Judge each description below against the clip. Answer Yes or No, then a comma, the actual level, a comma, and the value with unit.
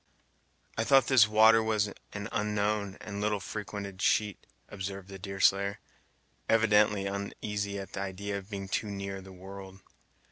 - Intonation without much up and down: Yes, narrow, 1.3 semitones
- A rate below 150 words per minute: Yes, average, 140 wpm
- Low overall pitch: Yes, low, 100 Hz